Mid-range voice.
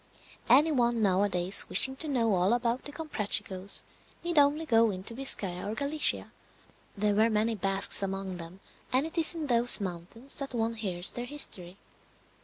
No: high, 225 Hz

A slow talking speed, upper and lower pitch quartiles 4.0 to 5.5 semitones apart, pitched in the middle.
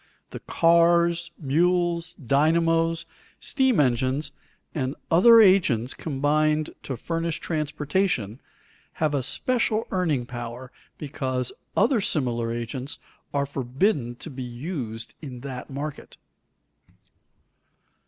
Yes: slow, 100 wpm; average, 4.7 semitones; medium, 150 Hz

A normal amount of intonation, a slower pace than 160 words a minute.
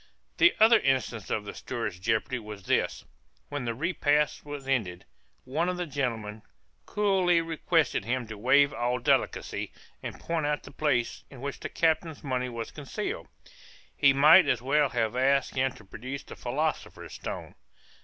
No: average, 4.4 semitones; average, 165 wpm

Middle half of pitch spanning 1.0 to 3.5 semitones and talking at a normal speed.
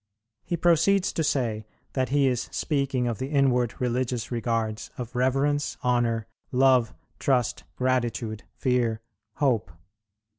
No: average, 2.7 semitones; slow, 120 wpm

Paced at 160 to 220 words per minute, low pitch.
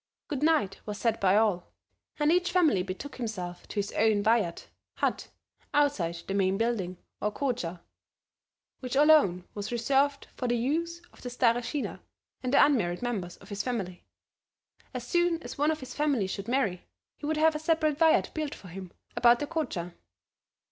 No: average, 170 wpm; high, 240 Hz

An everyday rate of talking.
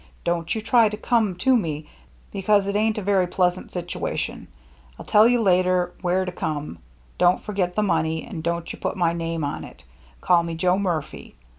Yes: average, 190 wpm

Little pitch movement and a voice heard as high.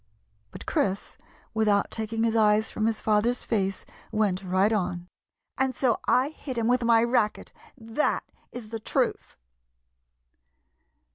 Yes: narrow, 2.2 semitones; high, 220 Hz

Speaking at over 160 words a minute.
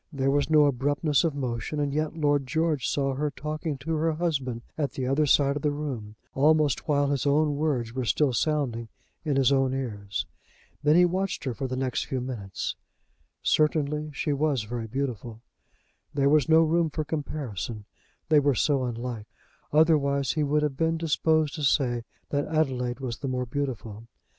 Yes: average, 180 wpm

